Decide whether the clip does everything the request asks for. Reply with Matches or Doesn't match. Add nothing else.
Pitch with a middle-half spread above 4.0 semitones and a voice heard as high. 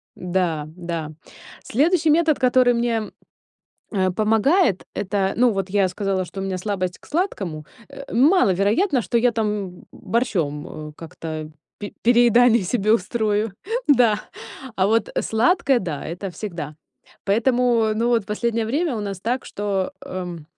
Matches